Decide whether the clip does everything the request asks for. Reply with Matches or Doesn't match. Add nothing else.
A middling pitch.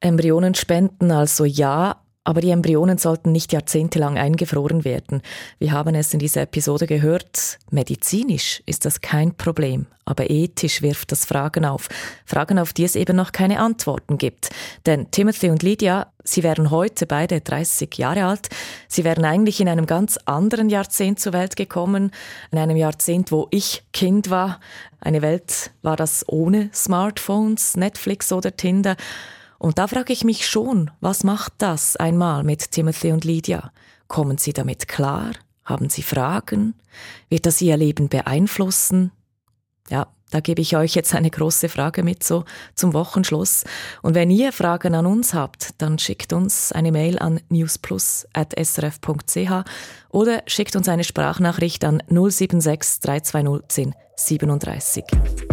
Matches